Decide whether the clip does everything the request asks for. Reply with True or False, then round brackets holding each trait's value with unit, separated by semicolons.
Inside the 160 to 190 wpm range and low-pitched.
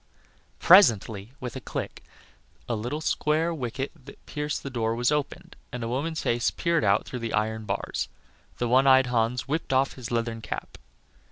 True (175 wpm; 125 Hz)